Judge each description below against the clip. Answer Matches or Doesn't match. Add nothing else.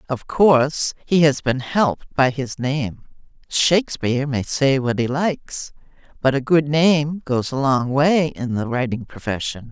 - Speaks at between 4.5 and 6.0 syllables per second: Doesn't match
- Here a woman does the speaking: Matches